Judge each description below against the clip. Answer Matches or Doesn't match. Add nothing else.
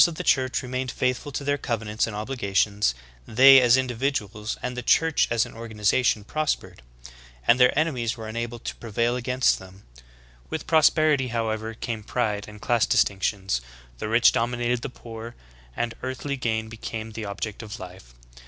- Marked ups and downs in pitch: Doesn't match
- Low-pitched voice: Matches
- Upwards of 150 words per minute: Matches